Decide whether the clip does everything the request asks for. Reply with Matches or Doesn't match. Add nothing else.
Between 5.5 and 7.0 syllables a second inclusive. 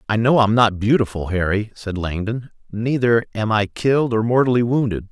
Doesn't match